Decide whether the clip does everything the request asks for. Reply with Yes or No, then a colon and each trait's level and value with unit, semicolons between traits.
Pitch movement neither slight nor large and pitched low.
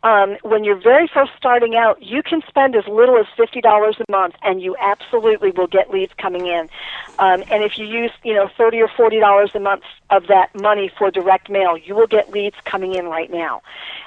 No: average, 3.2 semitones; high, 205 Hz